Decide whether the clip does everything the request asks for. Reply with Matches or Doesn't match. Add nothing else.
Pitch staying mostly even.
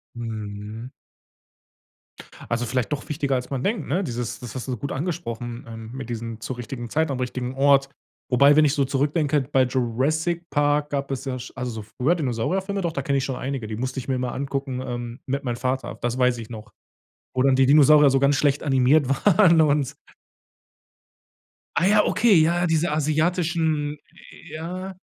Doesn't match